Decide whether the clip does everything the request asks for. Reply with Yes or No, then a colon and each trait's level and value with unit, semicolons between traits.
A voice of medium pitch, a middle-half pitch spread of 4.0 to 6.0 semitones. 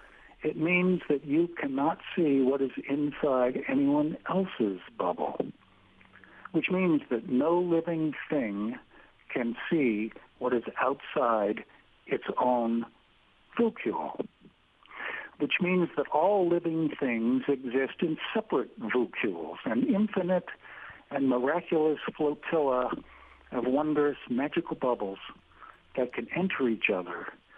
Yes: medium, 155 Hz; average, 5.3 semitones